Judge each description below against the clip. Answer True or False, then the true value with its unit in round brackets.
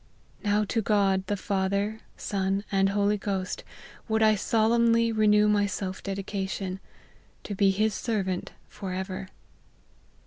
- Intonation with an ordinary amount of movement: False (1.8 semitones)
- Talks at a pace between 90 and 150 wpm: True (135 wpm)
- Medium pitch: False (200 Hz)